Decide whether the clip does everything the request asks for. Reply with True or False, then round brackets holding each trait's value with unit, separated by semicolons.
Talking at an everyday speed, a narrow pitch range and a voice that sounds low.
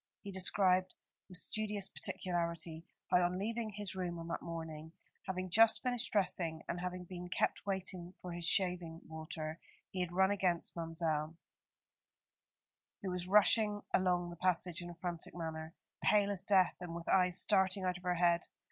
False (165 wpm; 2.0 semitones; 180 Hz)